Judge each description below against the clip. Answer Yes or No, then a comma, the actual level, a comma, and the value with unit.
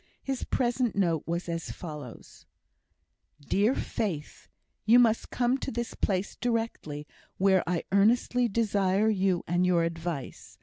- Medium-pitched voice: No, high, 195 Hz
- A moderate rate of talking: No, slow, 130 wpm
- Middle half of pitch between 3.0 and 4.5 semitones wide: No, average, 5.3 semitones